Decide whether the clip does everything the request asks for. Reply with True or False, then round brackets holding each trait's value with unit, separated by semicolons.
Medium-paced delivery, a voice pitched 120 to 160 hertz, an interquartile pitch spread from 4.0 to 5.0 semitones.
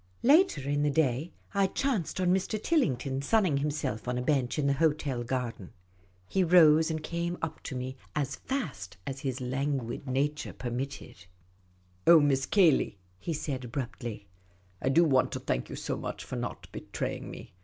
True (175 wpm; 140 Hz; 4.3 semitones)